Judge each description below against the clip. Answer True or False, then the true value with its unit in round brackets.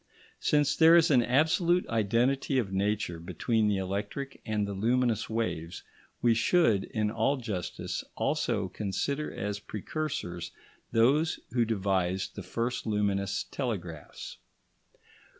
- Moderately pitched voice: False (110 Hz)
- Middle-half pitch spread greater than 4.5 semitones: True (5.2 semitones)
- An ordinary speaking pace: False (120 wpm)